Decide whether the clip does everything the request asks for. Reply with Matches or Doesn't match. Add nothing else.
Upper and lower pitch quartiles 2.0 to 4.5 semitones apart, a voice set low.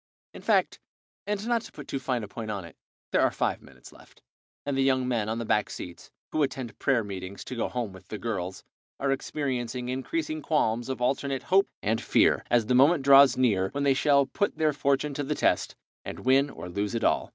Matches